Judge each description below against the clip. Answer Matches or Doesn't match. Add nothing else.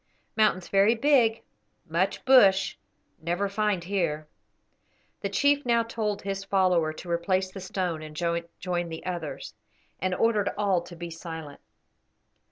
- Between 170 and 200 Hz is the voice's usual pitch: Matches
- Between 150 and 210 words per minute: Doesn't match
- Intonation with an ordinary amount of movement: Matches